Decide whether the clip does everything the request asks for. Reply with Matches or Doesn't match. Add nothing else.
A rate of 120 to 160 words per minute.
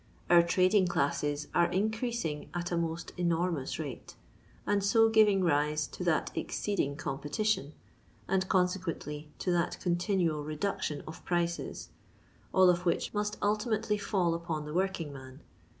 Matches